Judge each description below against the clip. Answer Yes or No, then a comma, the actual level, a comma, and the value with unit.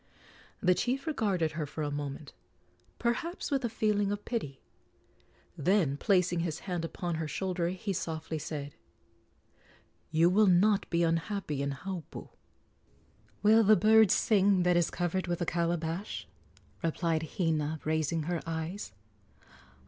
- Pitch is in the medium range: Yes, medium, 175 Hz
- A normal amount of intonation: Yes, average, 4.1 semitones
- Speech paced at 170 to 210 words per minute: No, slow, 135 wpm